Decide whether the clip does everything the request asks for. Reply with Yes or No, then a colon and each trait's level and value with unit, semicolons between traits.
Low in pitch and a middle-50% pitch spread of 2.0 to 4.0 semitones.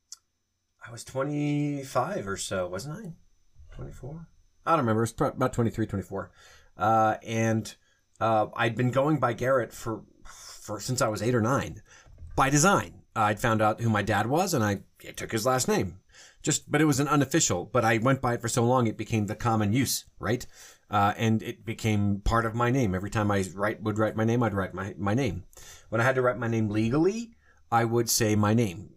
Yes: low, 115 Hz; average, 3.4 semitones